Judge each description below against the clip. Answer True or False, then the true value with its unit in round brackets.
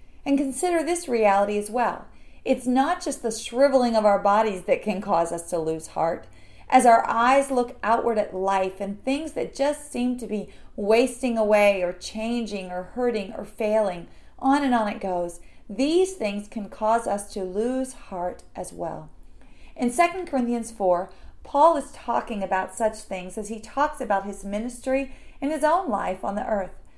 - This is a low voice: False (225 Hz)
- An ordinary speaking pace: True (180 wpm)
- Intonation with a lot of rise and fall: False (4.7 semitones)